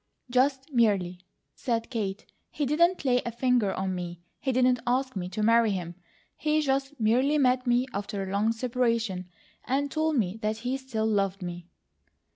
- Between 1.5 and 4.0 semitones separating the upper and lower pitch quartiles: No, average, 4.8 semitones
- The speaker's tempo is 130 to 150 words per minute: No, average, 170 wpm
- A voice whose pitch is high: Yes, high, 235 Hz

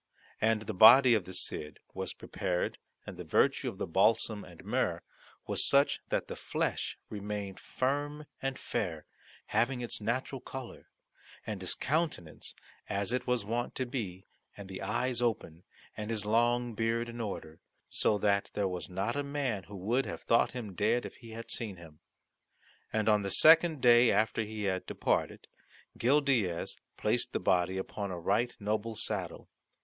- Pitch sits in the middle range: No, low, 110 Hz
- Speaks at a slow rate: No, average, 170 wpm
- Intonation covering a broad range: No, average, 3.8 semitones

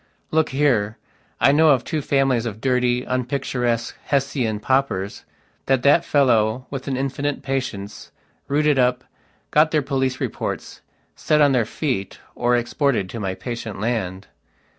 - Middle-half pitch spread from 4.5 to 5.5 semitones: No, average, 3.2 semitones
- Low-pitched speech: Yes, low, 130 Hz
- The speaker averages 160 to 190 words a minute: No, average, 140 wpm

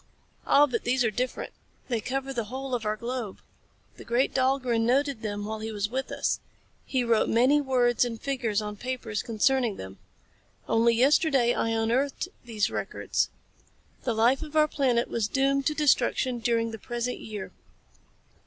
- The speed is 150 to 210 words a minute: Yes, average, 165 wpm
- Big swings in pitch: No, average, 3.0 semitones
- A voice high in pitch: Yes, high, 240 Hz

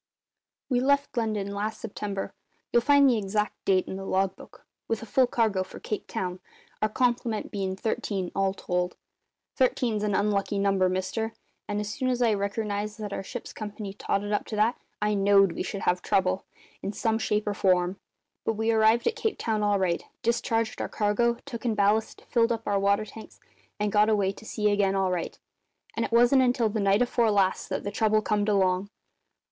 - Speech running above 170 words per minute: Yes, average, 195 wpm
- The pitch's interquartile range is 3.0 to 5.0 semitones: No, narrow, 2.4 semitones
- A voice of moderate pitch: No, high, 210 Hz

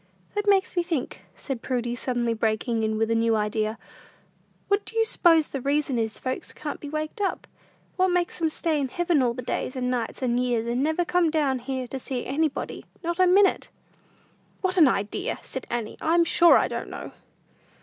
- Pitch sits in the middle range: No, very high, 275 Hz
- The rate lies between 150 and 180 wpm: No, average, 200 wpm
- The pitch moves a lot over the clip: Yes, wide, 6.1 semitones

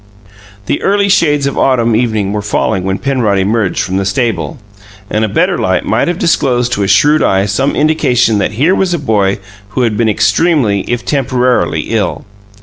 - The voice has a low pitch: Yes, low, 115 Hz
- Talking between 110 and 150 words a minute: No, average, 185 wpm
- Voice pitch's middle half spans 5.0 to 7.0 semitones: Yes, wide, 5.4 semitones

